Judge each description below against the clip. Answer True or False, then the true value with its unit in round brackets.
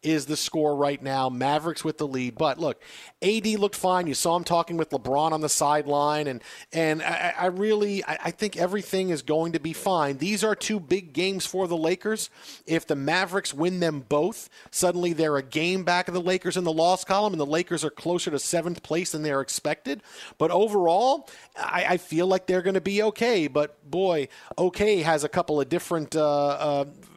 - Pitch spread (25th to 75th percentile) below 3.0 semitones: False (3.4 semitones)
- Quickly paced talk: True (210 wpm)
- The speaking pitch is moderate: True (170 Hz)